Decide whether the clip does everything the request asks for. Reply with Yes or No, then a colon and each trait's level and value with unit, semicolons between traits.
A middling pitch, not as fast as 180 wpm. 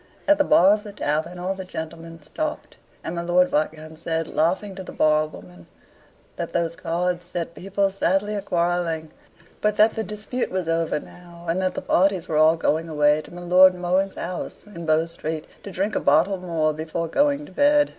No: medium, 175 Hz; average, 195 wpm